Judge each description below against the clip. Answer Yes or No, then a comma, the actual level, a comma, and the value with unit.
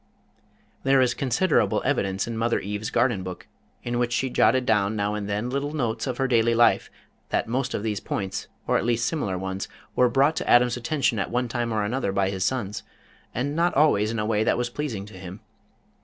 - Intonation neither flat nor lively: Yes, average, 3.8 semitones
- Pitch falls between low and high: No, low, 115 Hz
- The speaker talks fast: Yes, fast, 215 wpm